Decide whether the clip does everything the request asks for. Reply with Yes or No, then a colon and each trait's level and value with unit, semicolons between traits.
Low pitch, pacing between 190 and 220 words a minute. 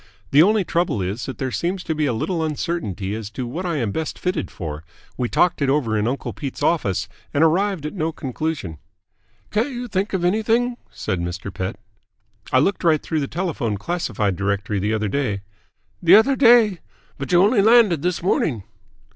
No: medium, 155 Hz; average, 195 wpm